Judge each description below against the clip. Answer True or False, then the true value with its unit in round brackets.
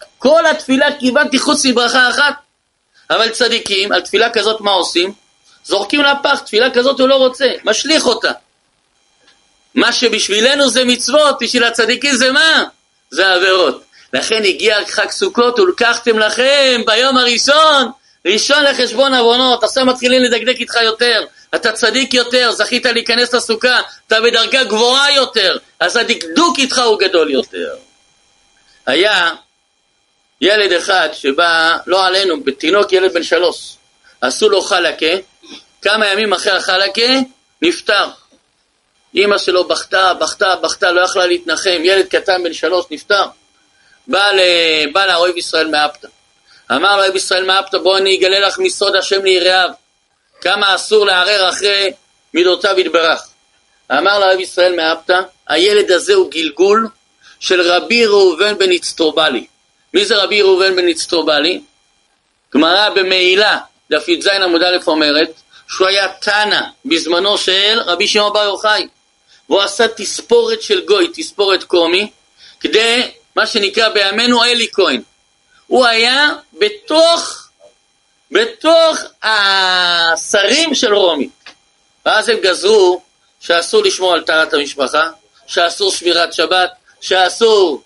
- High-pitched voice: True (220 Hz)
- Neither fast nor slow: True (125 wpm)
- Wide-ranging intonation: True (6.5 semitones)